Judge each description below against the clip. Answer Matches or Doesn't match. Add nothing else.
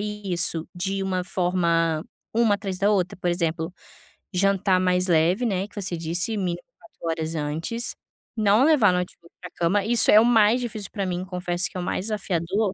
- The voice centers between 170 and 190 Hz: Matches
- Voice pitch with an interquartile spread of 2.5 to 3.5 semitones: Matches